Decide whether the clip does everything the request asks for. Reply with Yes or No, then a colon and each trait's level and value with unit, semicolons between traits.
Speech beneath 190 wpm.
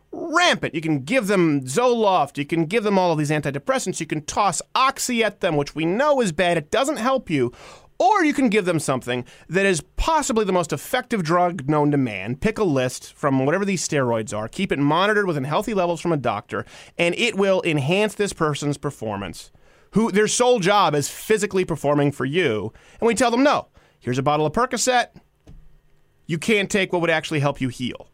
No: fast, 205 wpm